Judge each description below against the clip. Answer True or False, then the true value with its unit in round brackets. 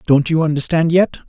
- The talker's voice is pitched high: False (160 Hz)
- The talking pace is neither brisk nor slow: True (190 wpm)